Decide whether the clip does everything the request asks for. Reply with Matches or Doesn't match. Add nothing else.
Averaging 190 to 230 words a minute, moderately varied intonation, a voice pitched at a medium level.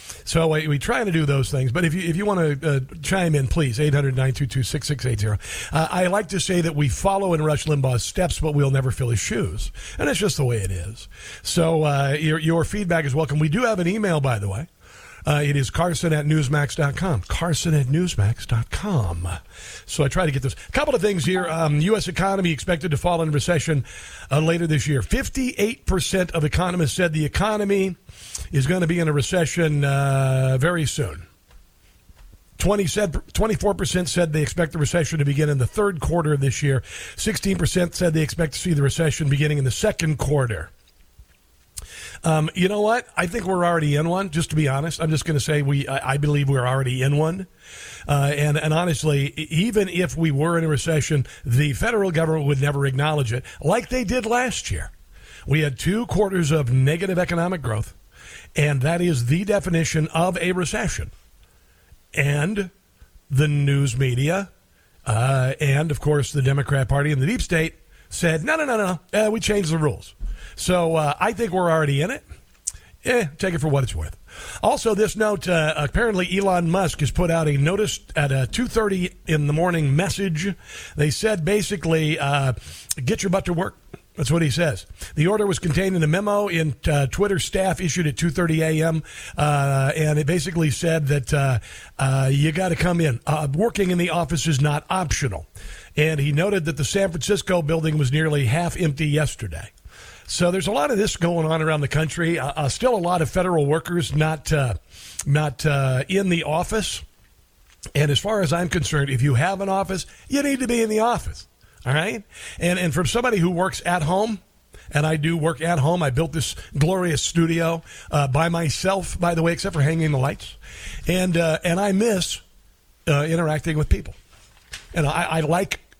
Matches